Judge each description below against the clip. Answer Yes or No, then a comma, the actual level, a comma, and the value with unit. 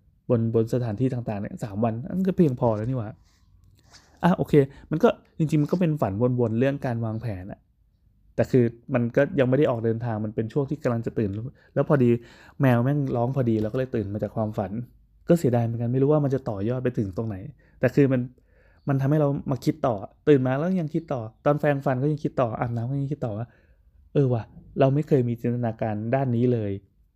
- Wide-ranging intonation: No, average, 3.9 semitones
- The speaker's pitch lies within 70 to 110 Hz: No, low, 125 Hz